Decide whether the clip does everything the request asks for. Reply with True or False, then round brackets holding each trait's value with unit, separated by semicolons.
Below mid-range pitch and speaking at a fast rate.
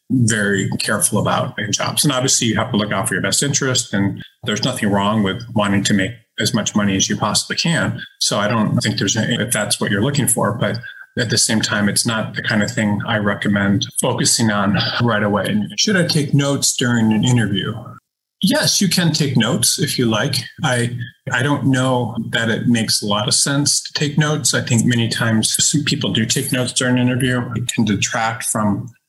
True (120 Hz; 215 wpm)